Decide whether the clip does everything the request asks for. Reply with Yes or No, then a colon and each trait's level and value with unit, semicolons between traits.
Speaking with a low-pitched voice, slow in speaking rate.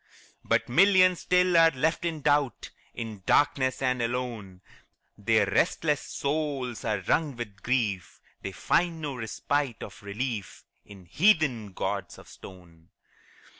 Yes: low, 125 Hz; slow, 130 wpm